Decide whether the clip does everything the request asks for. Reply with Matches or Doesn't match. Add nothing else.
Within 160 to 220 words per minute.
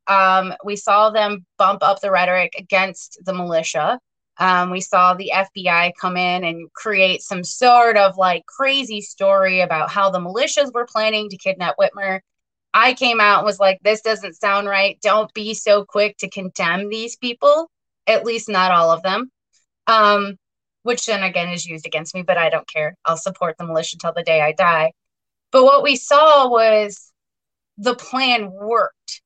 Matches